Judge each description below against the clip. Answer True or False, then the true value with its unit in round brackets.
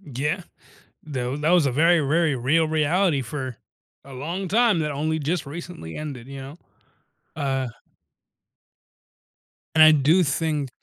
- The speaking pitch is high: False (150 Hz)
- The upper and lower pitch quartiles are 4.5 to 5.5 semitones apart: False (3.3 semitones)